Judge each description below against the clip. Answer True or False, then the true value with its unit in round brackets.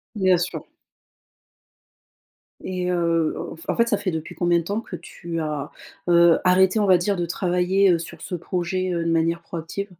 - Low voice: False (175 Hz)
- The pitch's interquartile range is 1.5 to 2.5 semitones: True (1.9 semitones)